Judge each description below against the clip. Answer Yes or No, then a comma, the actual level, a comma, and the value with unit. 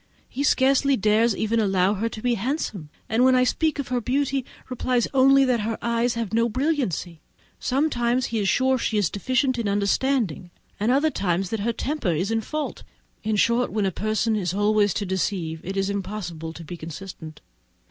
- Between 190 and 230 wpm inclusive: Yes, average, 195 wpm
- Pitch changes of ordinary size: Yes, average, 4.7 semitones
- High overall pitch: Yes, high, 225 Hz